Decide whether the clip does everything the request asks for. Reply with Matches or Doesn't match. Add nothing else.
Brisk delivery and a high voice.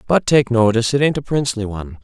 Doesn't match